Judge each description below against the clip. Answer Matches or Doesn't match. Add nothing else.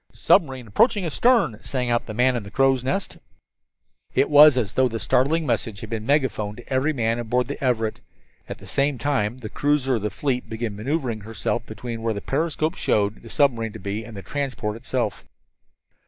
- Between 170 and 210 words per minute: Matches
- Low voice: Matches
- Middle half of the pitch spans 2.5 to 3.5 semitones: Doesn't match